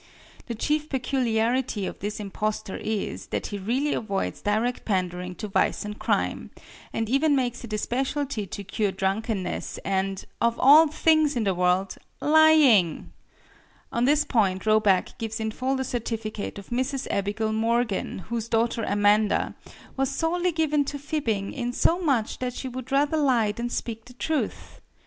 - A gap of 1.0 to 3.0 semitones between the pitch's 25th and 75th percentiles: No, average, 4.6 semitones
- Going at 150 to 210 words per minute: Yes, average, 160 wpm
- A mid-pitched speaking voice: No, high, 230 Hz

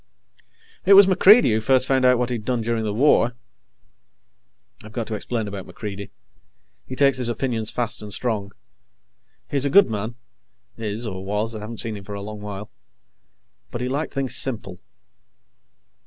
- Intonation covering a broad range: No, average, 3.5 semitones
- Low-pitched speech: Yes, low, 115 Hz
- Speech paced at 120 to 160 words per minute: No, average, 170 wpm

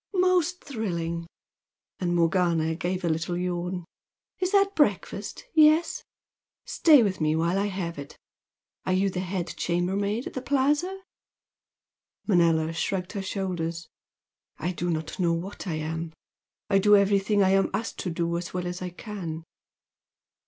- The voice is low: No, medium, 185 Hz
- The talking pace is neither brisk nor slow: Yes, average, 150 wpm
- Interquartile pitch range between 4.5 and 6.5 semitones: No, average, 3.5 semitones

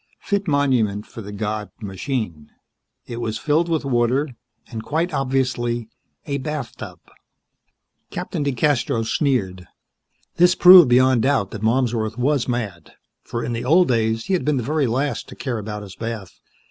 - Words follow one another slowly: No, average, 155 wpm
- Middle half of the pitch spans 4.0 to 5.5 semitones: Yes, average, 4.4 semitones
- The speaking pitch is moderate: No, low, 120 Hz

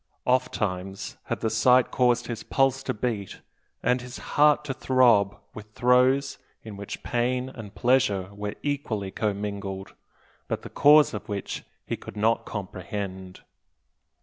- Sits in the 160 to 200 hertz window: No, low, 115 Hz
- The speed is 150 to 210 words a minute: No, average, 140 wpm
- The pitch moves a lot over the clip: No, average, 4.1 semitones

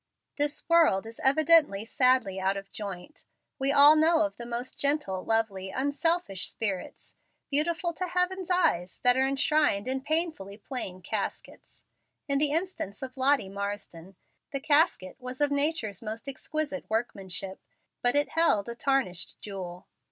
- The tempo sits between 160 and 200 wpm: No, average, 145 wpm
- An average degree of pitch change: No, wide, 7.2 semitones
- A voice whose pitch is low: No, very high, 260 Hz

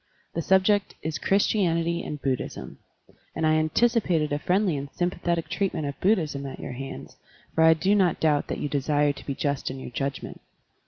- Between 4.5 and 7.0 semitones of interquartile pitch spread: No, average, 4.1 semitones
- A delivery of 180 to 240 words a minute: Yes, average, 190 wpm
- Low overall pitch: No, medium, 160 Hz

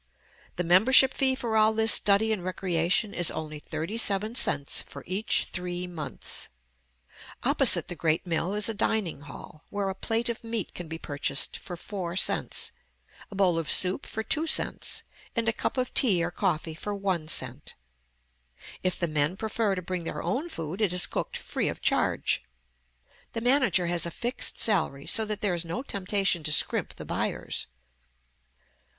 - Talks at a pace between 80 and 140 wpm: No, average, 175 wpm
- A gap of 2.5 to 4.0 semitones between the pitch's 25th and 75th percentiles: No, average, 4.7 semitones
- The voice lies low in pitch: No, high, 190 Hz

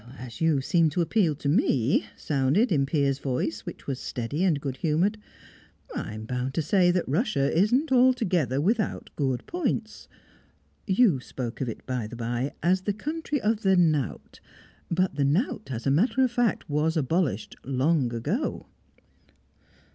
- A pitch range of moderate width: No, wide, 7.1 semitones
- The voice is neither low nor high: Yes, medium, 155 Hz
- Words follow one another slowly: No, average, 160 wpm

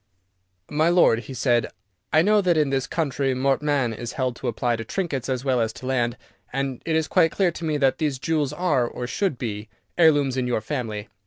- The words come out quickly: Yes, fast, 215 wpm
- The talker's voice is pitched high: No, low, 135 Hz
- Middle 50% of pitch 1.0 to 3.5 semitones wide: No, average, 4.3 semitones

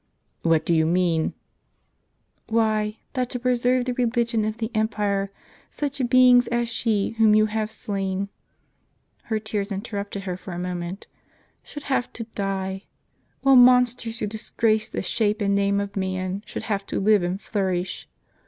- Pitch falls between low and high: No, high, 215 Hz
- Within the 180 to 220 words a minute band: No, average, 170 wpm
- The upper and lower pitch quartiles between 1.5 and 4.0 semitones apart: Yes, average, 3.3 semitones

